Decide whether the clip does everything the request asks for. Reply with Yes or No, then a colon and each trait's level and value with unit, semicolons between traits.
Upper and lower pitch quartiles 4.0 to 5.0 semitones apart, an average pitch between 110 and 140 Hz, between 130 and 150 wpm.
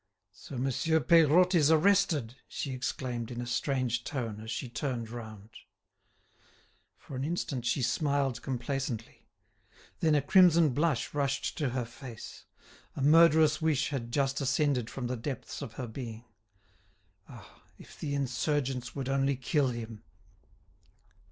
No: average, 3.6 semitones; low, 135 Hz; average, 140 wpm